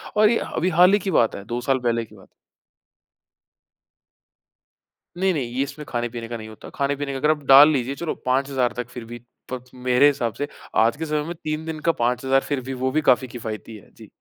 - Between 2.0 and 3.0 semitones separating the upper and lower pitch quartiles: No, average, 3.9 semitones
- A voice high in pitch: No, low, 135 Hz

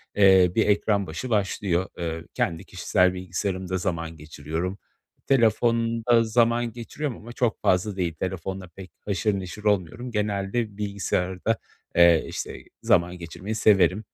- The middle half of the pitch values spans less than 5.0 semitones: Yes, average, 3.5 semitones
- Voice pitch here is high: No, very low, 95 Hz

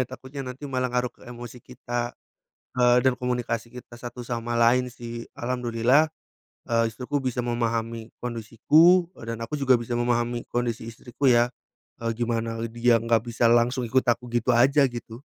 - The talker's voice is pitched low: Yes, low, 120 Hz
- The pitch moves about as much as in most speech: No, narrow, 1.3 semitones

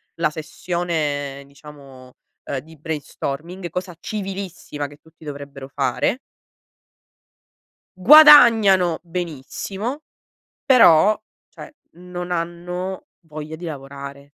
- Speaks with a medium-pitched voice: Yes, medium, 165 Hz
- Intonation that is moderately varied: Yes, average, 4.2 semitones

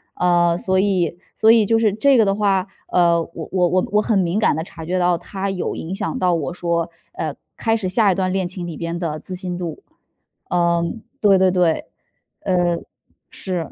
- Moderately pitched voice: Yes, medium, 180 Hz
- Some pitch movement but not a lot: No, narrow, 2.3 semitones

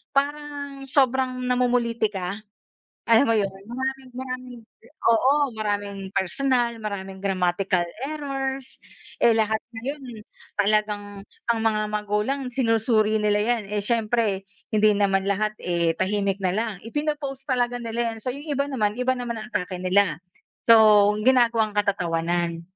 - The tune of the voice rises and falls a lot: No, average, 3.9 semitones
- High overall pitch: Yes, high, 225 Hz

